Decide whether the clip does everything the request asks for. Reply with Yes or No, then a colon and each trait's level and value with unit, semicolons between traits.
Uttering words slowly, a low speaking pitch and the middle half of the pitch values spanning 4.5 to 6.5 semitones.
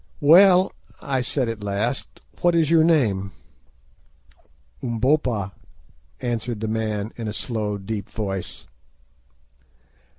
Yes: slow, 105 wpm; low, 115 Hz; average, 4.8 semitones